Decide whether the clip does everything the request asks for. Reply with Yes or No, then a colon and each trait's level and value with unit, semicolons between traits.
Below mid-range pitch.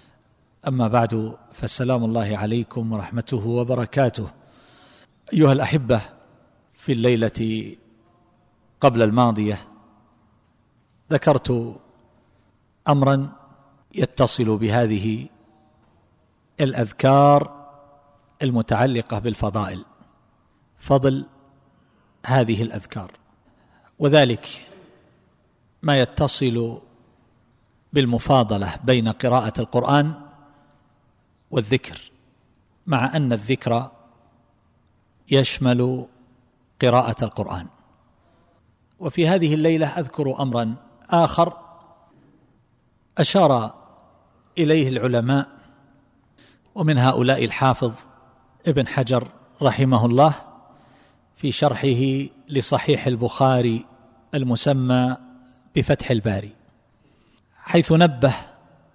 Yes: low, 125 Hz